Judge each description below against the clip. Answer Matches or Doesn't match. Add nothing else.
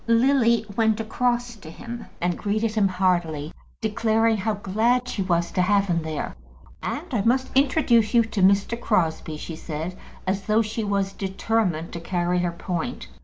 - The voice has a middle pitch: Doesn't match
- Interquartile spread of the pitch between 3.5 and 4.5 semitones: Matches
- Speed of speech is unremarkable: Matches